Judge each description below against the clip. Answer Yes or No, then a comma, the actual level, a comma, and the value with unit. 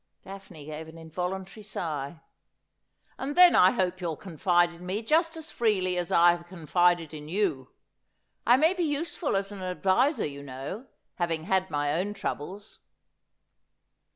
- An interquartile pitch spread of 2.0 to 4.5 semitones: Yes, average, 4.2 semitones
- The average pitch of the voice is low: No, medium, 180 Hz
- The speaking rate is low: No, average, 155 wpm